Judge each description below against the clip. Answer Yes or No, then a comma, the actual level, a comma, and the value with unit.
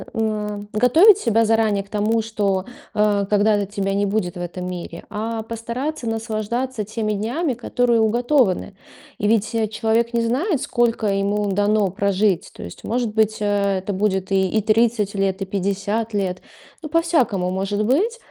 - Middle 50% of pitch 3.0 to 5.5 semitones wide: No, narrow, 2.5 semitones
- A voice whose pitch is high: Yes, high, 215 Hz